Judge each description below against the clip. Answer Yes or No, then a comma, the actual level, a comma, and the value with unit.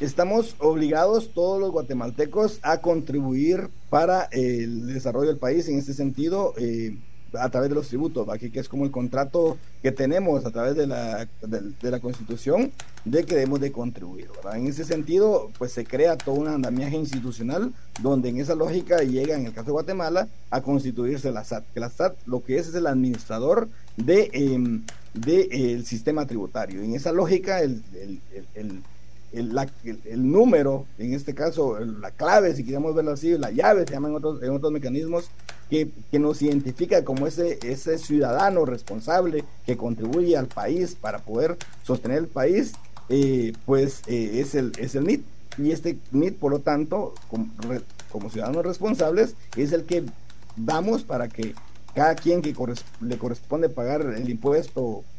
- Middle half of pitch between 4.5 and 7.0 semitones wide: Yes, average, 5.0 semitones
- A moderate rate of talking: Yes, average, 180 wpm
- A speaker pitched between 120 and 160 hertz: Yes, low, 135 Hz